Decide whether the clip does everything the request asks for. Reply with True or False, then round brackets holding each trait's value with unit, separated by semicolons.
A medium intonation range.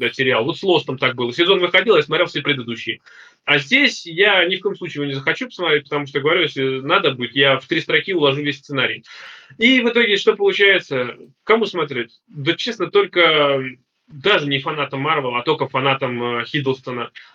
False (5.8 semitones)